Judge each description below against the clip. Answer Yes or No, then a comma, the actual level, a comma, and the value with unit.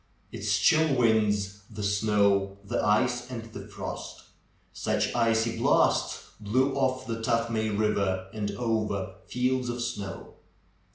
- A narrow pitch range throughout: No, average, 3.0 semitones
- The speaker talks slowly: Yes, slow, 125 wpm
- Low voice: Yes, low, 110 Hz